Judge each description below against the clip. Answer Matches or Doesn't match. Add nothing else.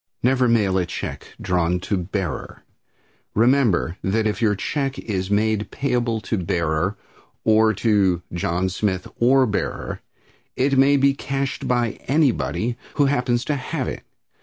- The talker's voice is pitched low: Matches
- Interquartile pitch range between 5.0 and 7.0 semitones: Matches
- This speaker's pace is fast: Doesn't match